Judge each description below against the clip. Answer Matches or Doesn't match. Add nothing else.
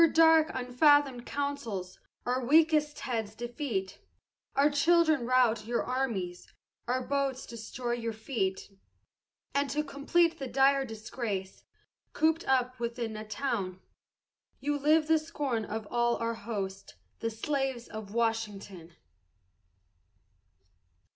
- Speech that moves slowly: Matches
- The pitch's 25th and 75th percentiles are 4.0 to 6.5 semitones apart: Matches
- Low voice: Doesn't match